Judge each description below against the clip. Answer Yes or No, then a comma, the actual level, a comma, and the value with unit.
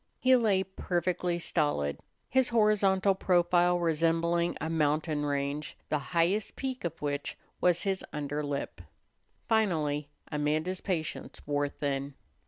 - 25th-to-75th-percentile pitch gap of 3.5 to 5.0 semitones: Yes, average, 4.3 semitones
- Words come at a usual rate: No, slow, 120 wpm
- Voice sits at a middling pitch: Yes, medium, 165 Hz